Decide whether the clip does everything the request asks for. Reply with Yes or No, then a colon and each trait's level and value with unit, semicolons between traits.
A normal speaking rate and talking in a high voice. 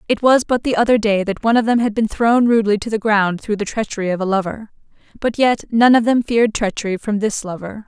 No: fast, 250 wpm; high, 220 Hz